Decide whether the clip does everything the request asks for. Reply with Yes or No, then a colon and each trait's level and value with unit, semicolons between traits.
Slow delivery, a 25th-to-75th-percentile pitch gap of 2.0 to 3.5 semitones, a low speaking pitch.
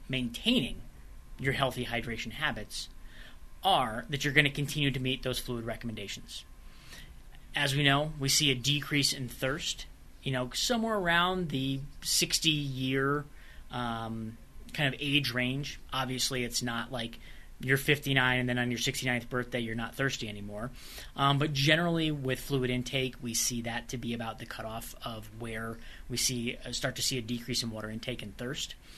No: average, 170 wpm; average, 3.1 semitones; low, 125 Hz